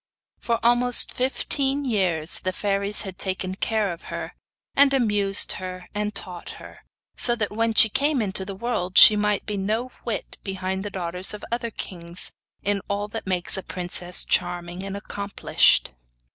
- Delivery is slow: No, average, 165 wpm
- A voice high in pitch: Yes, high, 200 Hz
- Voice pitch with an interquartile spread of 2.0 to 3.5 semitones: Yes, average, 3.2 semitones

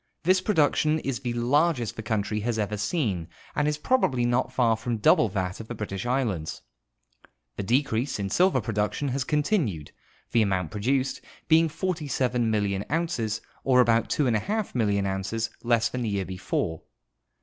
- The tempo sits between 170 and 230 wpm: No, average, 155 wpm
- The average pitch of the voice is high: No, low, 120 Hz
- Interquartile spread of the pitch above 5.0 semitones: Yes, wide, 5.4 semitones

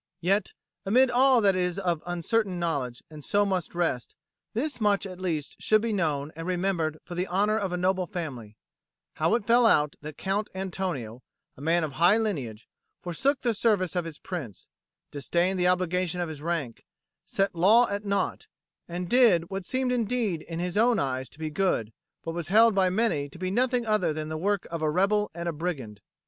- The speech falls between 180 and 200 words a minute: Yes, average, 195 wpm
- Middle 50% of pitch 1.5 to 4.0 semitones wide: No, average, 4.5 semitones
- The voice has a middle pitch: Yes, medium, 180 Hz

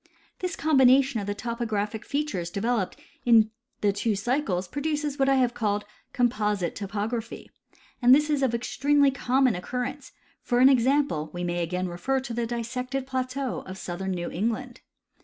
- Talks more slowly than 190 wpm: Yes, average, 170 wpm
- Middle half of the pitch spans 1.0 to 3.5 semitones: No, average, 4.8 semitones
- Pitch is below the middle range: No, high, 240 Hz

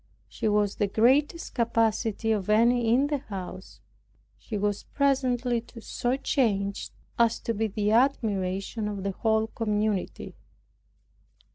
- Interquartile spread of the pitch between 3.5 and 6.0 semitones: No, average, 2.9 semitones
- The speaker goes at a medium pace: No, slow, 125 wpm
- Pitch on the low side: No, high, 220 Hz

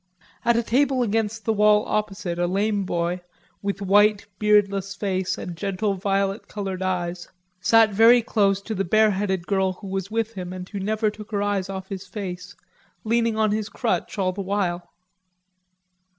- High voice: Yes, high, 200 Hz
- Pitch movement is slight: Yes, narrow, 2.3 semitones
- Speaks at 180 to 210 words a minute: No, average, 170 wpm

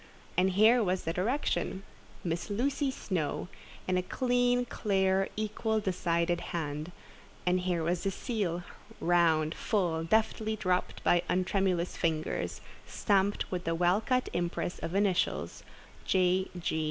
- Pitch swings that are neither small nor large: Yes, average, 3.6 semitones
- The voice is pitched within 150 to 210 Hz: Yes, medium, 185 Hz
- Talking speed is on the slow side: Yes, slow, 130 wpm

